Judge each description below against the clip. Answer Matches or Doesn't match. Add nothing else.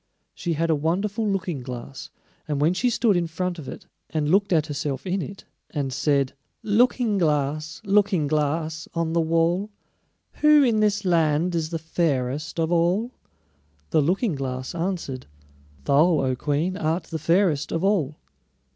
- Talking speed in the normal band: Matches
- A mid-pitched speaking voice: Matches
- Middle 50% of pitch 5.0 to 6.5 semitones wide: Doesn't match